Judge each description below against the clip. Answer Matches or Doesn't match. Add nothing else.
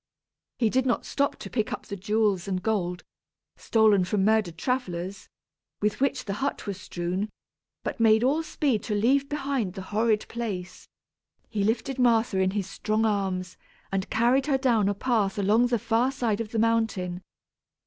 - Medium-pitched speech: Doesn't match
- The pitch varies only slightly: Doesn't match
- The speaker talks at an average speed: Matches